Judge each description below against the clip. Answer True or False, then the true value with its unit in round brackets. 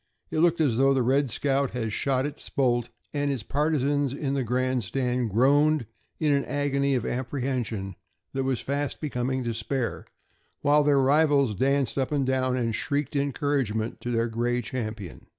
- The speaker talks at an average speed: True (165 wpm)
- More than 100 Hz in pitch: True (135 Hz)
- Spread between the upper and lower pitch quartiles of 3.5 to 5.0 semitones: False (2.8 semitones)